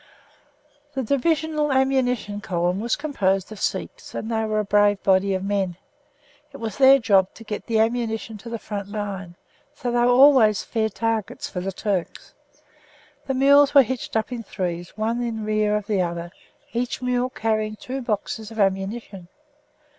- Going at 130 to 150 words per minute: No, average, 175 wpm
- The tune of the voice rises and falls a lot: No, average, 3.7 semitones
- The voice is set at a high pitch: Yes, high, 220 Hz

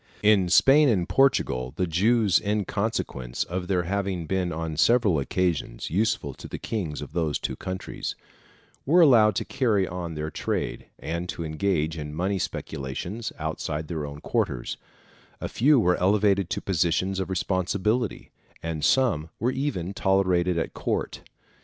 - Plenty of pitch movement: No, average, 4.5 semitones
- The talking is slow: No, average, 155 wpm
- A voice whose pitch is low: Yes, very low, 90 Hz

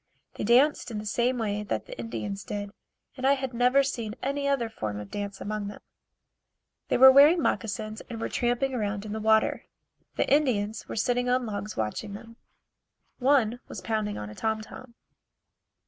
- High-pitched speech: Yes, high, 225 Hz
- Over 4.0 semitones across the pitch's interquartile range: No, average, 3.5 semitones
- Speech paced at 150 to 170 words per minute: No, average, 180 wpm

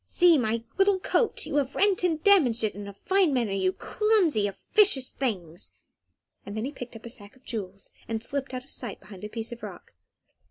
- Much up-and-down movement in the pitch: Yes, wide, 7.5 semitones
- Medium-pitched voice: No, high, 245 Hz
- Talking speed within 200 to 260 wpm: Yes, fast, 205 wpm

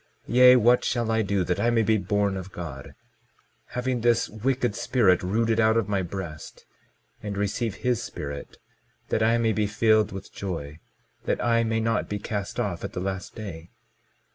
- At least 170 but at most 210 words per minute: Yes, average, 180 wpm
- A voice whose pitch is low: Yes, low, 105 Hz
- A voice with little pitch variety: No, average, 3.3 semitones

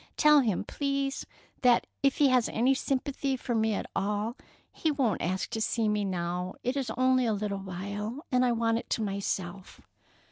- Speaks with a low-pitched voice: No, high, 230 Hz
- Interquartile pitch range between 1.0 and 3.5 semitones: No, average, 4.6 semitones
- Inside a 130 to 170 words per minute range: No, average, 185 wpm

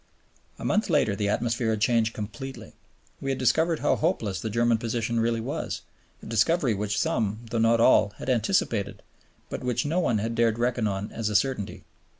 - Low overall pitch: Yes, low, 115 Hz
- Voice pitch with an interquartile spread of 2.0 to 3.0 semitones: Yes, average, 2.7 semitones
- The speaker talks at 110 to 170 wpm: No, average, 185 wpm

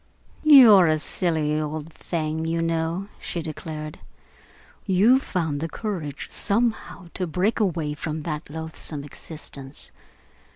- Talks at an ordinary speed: No, slow, 120 wpm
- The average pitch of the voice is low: No, medium, 160 Hz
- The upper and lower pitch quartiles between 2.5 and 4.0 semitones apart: Yes, average, 3.3 semitones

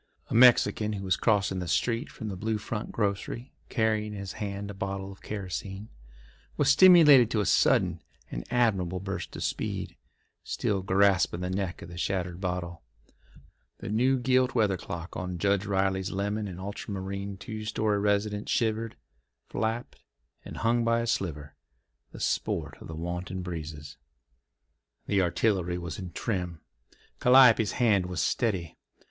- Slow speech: No, average, 155 wpm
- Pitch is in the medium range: No, low, 100 Hz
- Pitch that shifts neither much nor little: Yes, average, 3.3 semitones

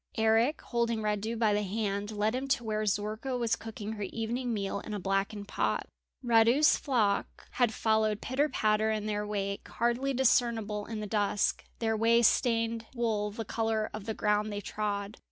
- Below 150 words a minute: No, average, 175 wpm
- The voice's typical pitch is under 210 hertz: No, high, 220 Hz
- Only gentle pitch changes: Yes, narrow, 2.0 semitones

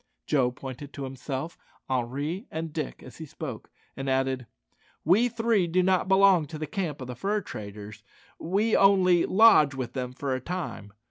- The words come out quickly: No, average, 175 wpm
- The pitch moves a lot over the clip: Yes, wide, 6.0 semitones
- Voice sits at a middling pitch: Yes, medium, 150 Hz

